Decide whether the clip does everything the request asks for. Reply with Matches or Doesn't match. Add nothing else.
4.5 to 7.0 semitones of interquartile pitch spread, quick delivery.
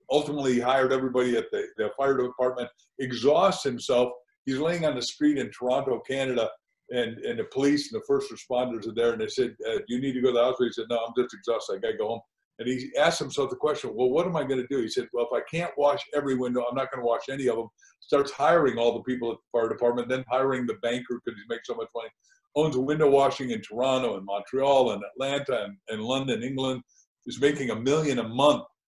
Matches